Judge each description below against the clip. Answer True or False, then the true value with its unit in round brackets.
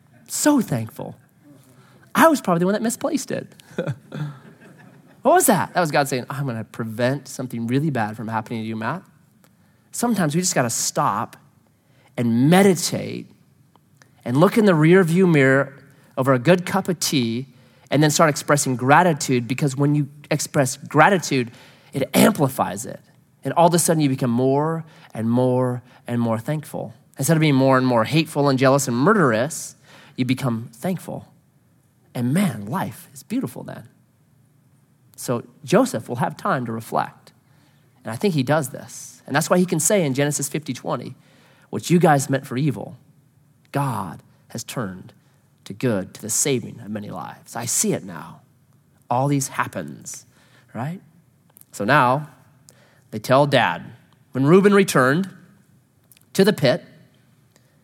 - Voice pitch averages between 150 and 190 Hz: False (140 Hz)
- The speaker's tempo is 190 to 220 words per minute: False (160 wpm)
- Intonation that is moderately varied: True (4.0 semitones)